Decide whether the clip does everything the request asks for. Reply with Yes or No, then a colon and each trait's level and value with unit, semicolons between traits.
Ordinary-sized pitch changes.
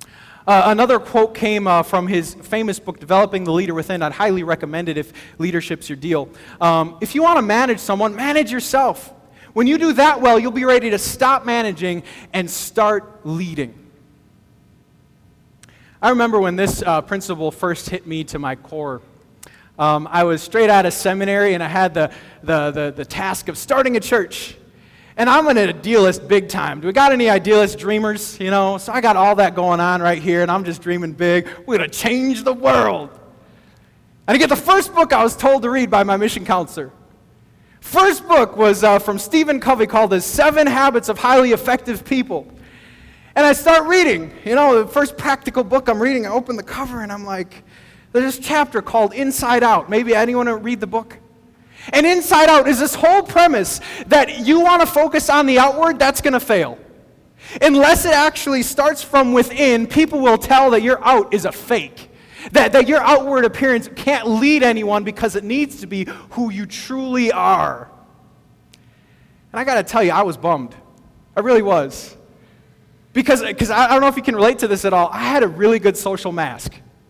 No: wide, 6.2 semitones